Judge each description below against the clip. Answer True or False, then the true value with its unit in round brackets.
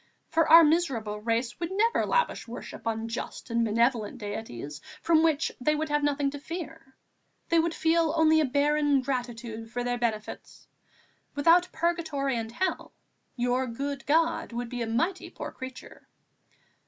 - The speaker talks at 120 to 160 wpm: True (155 wpm)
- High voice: True (275 Hz)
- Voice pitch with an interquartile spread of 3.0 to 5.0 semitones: False (5.5 semitones)